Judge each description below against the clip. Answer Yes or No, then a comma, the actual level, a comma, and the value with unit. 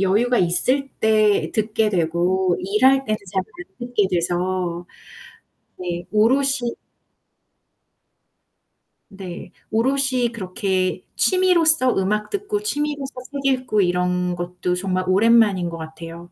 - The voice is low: No, high, 205 Hz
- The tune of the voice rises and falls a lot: Yes, wide, 6.2 semitones